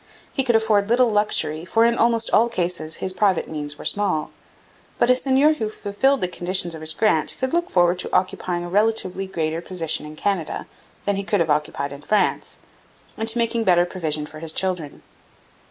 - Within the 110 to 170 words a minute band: No, average, 195 wpm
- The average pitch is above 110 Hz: Yes, medium, 185 Hz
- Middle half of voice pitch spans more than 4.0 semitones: Yes, wide, 5.4 semitones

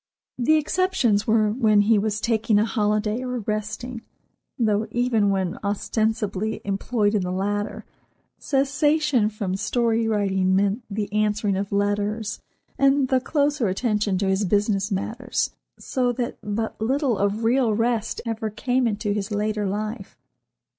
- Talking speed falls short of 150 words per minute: Yes, average, 140 wpm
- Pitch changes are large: No, average, 2.8 semitones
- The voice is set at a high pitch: Yes, high, 215 Hz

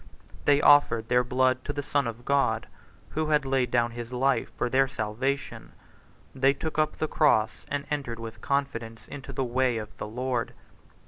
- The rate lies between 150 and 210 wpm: Yes, average, 180 wpm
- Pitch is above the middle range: No, low, 130 Hz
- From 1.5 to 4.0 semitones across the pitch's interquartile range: Yes, average, 3.0 semitones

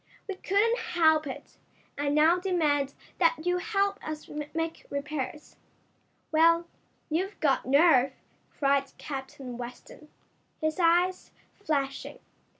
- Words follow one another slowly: Yes, slow, 110 wpm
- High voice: Yes, very high, 315 Hz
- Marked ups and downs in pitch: No, average, 4.1 semitones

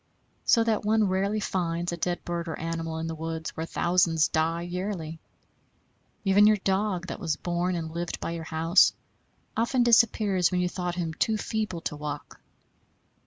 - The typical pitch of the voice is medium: Yes, medium, 175 Hz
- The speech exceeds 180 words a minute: No, average, 170 wpm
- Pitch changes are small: No, average, 3.3 semitones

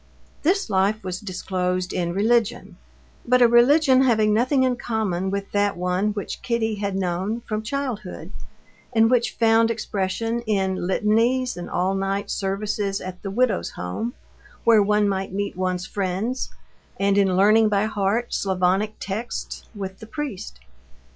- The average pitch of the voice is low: No, high, 205 Hz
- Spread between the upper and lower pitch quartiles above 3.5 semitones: No, average, 3.2 semitones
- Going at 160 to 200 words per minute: No, average, 145 wpm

